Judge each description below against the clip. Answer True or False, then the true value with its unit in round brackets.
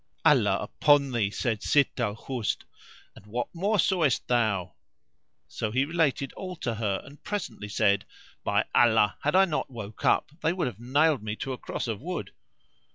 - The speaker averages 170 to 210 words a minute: True (175 wpm)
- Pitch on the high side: False (125 Hz)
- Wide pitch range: True (6.1 semitones)